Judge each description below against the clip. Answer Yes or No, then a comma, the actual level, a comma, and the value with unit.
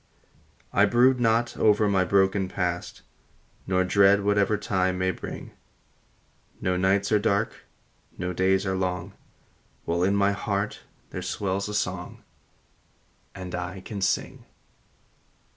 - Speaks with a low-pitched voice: Yes, very low, 95 Hz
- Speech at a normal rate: No, slow, 125 wpm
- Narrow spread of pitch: Yes, narrow, 1.7 semitones